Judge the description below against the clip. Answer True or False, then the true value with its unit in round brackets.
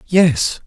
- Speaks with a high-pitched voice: False (175 Hz)